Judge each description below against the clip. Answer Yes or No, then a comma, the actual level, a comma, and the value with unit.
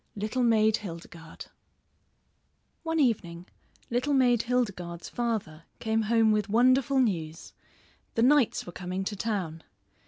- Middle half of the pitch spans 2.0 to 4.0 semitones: No, average, 5.3 semitones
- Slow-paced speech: Yes, slow, 120 wpm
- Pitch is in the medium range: No, high, 220 Hz